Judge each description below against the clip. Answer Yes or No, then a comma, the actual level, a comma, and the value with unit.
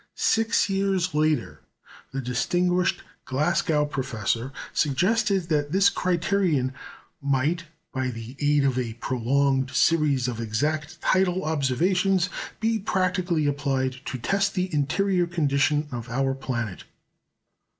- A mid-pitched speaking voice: Yes, medium, 150 Hz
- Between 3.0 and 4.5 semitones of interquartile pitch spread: No, wide, 5.5 semitones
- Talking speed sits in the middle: No, slow, 115 wpm